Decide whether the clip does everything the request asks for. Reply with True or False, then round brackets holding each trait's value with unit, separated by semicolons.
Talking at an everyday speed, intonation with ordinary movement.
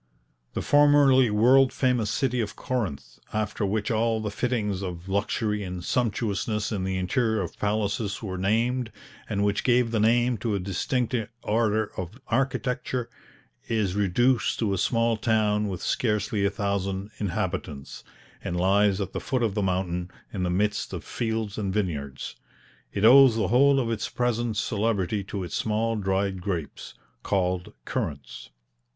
True (155 wpm; 3.2 semitones)